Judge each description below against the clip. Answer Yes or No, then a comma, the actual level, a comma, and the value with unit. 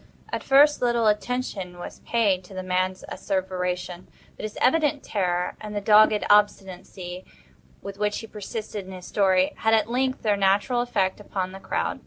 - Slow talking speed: No, average, 170 wpm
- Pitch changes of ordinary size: Yes, average, 3.1 semitones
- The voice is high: Yes, high, 205 Hz